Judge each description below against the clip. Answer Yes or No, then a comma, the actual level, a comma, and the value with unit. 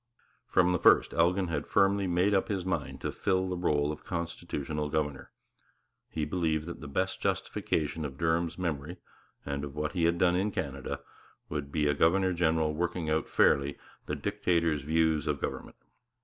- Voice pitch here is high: No, very low, 80 Hz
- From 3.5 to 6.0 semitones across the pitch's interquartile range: No, average, 3.0 semitones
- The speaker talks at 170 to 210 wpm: Yes, average, 175 wpm